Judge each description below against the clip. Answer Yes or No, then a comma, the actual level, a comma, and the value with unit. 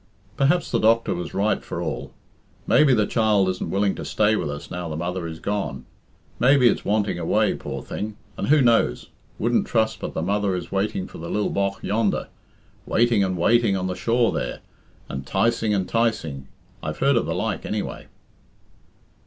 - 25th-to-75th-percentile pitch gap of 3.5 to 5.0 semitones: Yes, average, 4.1 semitones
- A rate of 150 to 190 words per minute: Yes, average, 185 wpm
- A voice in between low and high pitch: No, low, 105 Hz